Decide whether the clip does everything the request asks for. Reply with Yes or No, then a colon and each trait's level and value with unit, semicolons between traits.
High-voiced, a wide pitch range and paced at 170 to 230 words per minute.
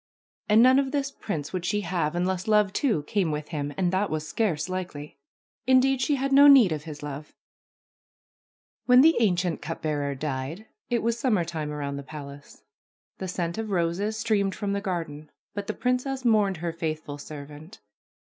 No: medium, 180 Hz; wide, 6.4 semitones; average, 175 wpm